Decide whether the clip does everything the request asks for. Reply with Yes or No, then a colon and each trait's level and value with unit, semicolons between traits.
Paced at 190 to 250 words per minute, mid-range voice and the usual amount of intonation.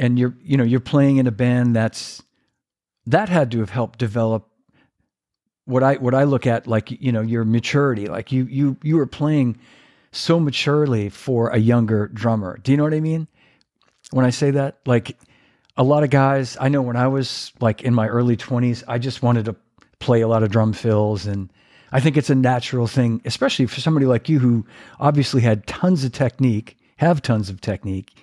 No: fast, 205 wpm; low, 125 Hz; average, 3.2 semitones